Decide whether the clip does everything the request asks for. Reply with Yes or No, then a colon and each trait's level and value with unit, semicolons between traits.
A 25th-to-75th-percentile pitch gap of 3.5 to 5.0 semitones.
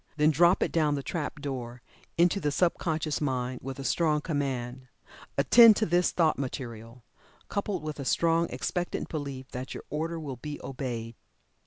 Yes: average, 4.3 semitones